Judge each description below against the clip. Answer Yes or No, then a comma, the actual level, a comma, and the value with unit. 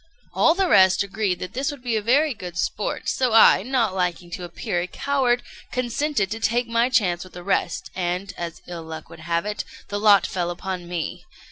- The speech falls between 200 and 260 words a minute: Yes, fast, 205 wpm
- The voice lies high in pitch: Yes, high, 200 Hz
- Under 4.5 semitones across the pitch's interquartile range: No, wide, 5.4 semitones